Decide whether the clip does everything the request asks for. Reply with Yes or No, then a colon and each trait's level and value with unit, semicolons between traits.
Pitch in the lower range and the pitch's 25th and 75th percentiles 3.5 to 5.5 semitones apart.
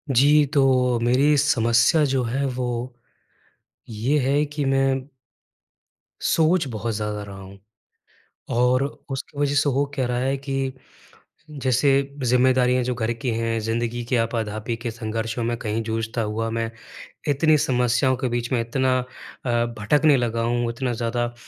No: low, 125 Hz; average, 2.8 semitones